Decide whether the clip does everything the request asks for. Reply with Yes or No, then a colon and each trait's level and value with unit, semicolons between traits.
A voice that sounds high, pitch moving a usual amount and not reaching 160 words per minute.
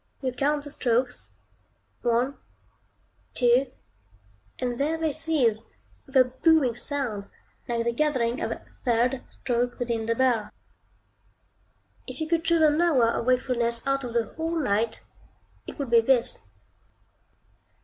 Yes: very high, 250 Hz; average, 3.5 semitones; average, 140 wpm